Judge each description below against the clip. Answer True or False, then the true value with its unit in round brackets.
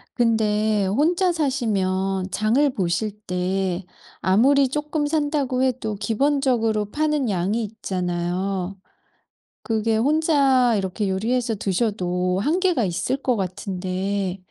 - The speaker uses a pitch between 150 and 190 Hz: False (215 Hz)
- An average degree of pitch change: False (5.9 semitones)